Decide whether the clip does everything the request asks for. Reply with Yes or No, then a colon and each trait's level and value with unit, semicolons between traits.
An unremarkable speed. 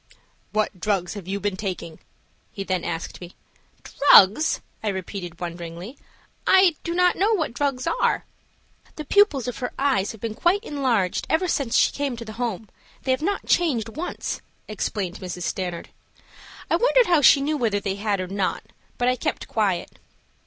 Yes: average, 170 wpm